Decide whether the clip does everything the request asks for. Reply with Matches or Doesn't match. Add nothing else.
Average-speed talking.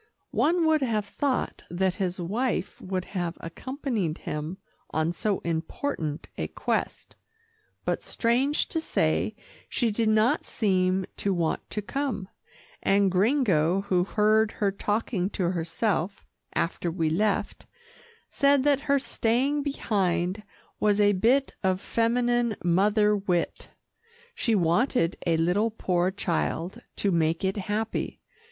Doesn't match